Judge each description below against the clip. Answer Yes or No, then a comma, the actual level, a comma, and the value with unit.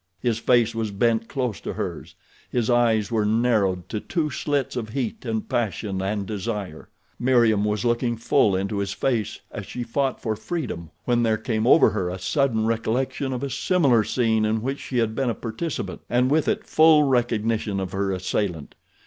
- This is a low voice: Yes, low, 115 Hz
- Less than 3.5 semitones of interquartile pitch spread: Yes, average, 2.9 semitones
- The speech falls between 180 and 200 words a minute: Yes, average, 185 wpm